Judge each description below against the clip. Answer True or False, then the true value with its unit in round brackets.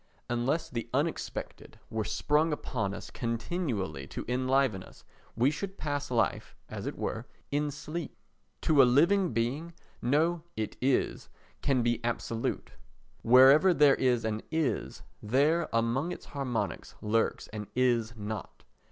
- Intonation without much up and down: False (4.5 semitones)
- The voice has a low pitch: True (130 Hz)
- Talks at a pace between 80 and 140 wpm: True (135 wpm)